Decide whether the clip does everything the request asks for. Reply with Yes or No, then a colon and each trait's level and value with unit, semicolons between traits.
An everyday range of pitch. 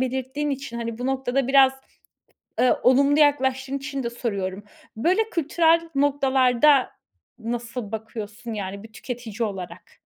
Yes: average, 3.3 semitones